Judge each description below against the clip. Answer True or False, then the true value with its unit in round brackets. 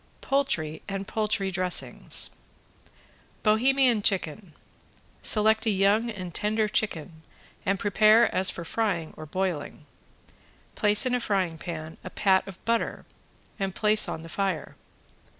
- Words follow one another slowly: True (130 wpm)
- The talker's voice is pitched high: True (195 Hz)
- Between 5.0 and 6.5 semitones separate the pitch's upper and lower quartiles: False (3.5 semitones)